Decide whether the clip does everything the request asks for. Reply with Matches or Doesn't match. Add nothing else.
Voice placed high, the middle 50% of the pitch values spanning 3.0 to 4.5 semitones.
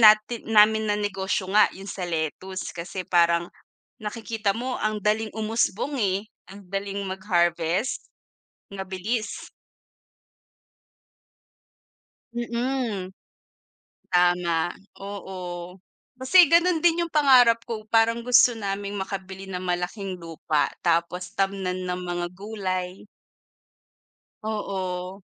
Matches